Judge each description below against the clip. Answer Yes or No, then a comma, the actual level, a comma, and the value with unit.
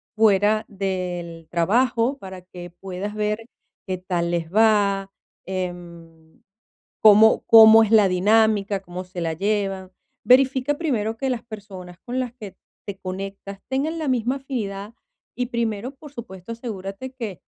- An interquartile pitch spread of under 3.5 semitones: No, average, 3.8 semitones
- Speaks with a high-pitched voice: Yes, high, 205 Hz